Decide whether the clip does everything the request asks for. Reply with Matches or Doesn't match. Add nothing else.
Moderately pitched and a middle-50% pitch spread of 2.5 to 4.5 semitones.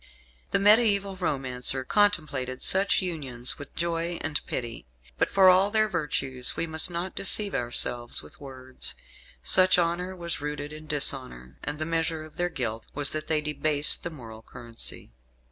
Doesn't match